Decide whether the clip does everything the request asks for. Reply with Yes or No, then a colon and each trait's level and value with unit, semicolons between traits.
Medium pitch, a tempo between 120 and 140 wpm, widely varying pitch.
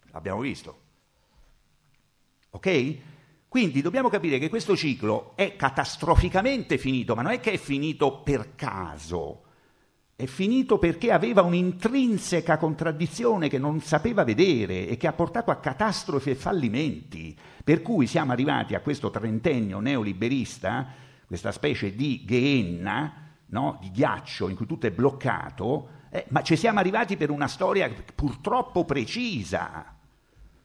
Yes: medium, 150 Hz; average, 135 wpm; wide, 6.2 semitones